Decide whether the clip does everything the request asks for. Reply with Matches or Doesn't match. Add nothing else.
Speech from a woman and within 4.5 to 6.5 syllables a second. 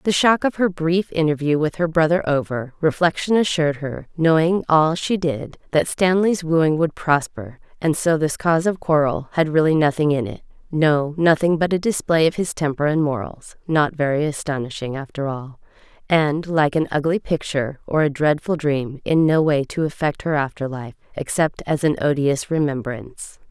Matches